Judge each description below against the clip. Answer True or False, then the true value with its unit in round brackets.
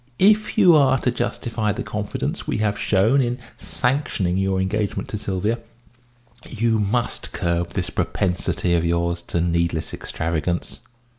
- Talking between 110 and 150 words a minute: True (140 wpm)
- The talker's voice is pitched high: False (100 Hz)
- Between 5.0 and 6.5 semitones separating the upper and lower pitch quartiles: True (5.5 semitones)